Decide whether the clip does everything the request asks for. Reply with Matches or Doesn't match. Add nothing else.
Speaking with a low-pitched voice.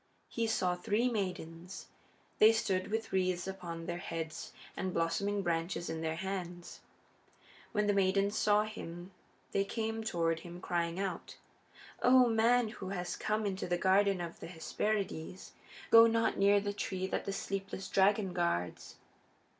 Doesn't match